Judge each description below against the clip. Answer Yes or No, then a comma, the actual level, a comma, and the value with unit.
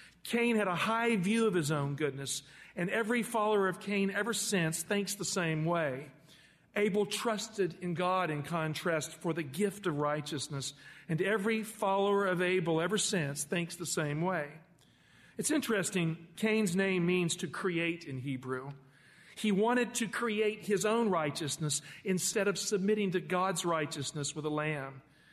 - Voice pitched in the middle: Yes, medium, 180 Hz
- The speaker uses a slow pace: No, average, 160 wpm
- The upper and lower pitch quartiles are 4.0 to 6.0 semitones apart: Yes, average, 4.9 semitones